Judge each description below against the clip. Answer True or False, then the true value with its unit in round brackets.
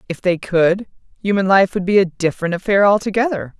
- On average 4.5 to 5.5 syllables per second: False (5.8 syllables/s)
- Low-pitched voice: False (190 Hz)